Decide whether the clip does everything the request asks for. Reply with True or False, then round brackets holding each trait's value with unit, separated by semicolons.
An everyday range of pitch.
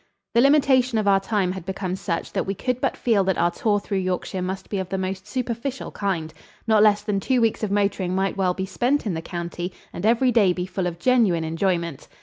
True (3.5 semitones)